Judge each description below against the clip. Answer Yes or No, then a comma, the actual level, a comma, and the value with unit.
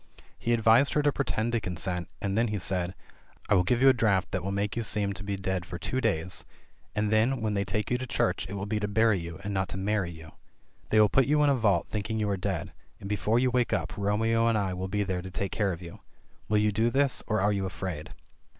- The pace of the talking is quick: Yes, fast, 270 wpm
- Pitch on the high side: No, low, 105 Hz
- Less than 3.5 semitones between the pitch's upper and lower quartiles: Yes, average, 3.1 semitones